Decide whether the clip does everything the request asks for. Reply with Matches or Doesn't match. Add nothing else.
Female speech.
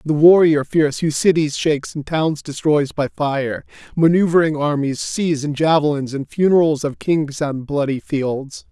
Doesn't match